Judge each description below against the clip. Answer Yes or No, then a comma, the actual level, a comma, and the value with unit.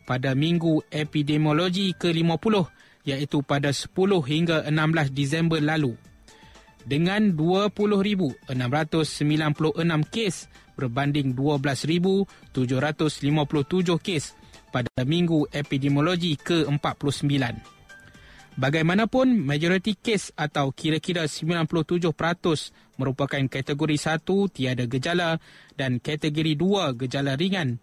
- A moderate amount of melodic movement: Yes, average, 3.2 semitones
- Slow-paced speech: Yes, slow, 80 wpm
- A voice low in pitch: No, medium, 155 Hz